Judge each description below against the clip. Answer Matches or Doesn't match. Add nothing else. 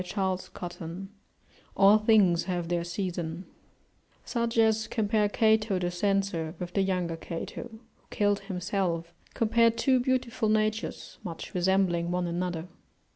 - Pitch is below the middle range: Doesn't match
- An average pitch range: Matches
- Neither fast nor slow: Doesn't match